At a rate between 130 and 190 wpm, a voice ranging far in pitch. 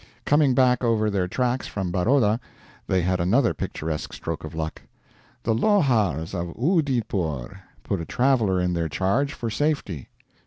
Yes: average, 150 wpm; wide, 6.6 semitones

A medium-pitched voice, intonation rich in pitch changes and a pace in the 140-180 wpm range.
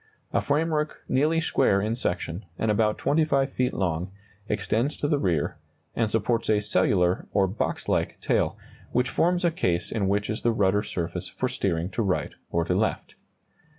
No: low, 110 Hz; wide, 6.2 semitones; average, 175 wpm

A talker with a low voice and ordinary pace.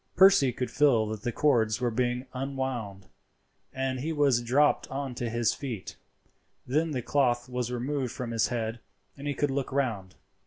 Yes: low, 125 Hz; average, 170 wpm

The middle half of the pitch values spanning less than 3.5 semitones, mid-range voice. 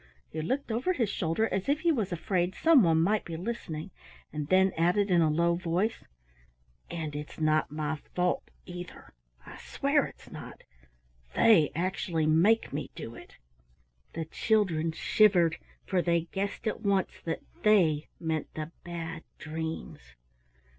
No: average, 4.0 semitones; medium, 170 Hz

